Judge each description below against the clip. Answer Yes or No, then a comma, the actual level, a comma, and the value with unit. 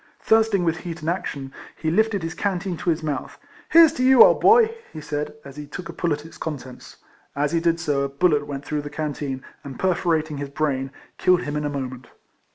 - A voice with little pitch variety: No, average, 3.5 semitones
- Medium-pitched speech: Yes, medium, 155 Hz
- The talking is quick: Yes, fast, 235 wpm